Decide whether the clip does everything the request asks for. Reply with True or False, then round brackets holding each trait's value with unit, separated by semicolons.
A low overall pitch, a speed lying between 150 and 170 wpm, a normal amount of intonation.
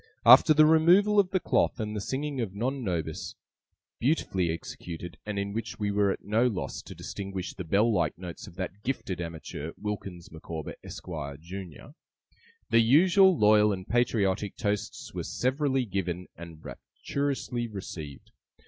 False (105 Hz; 155 wpm; 6.0 semitones)